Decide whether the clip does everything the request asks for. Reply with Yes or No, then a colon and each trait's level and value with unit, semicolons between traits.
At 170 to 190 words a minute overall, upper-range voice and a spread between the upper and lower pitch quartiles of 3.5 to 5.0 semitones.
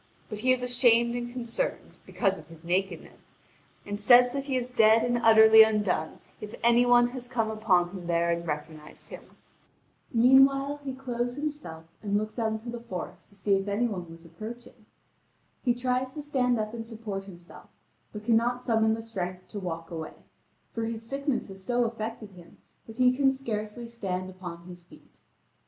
Yes: average, 180 wpm; high, 225 Hz; average, 4.2 semitones